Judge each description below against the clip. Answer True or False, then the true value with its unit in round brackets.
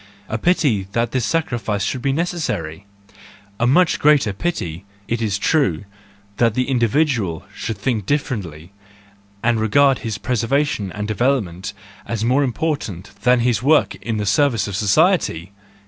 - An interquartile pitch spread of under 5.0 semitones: False (5.4 semitones)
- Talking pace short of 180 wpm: True (145 wpm)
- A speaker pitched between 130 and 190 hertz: False (115 Hz)